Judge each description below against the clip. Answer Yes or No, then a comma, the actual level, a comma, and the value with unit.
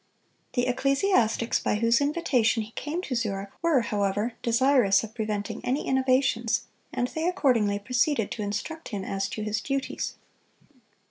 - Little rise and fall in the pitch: No, average, 4.5 semitones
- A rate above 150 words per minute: No, average, 145 wpm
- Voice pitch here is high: Yes, high, 235 Hz